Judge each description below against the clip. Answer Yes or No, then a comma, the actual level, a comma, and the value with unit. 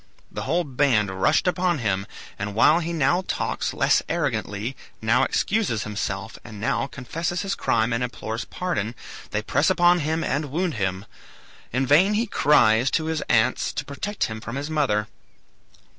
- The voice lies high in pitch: No, low, 135 Hz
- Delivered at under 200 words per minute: Yes, average, 165 wpm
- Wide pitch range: Yes, wide, 6.9 semitones